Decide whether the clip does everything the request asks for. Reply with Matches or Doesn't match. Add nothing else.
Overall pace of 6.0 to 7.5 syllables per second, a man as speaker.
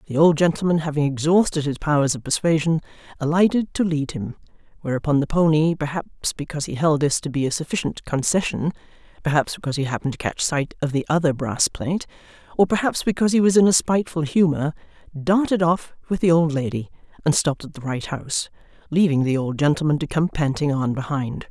Doesn't match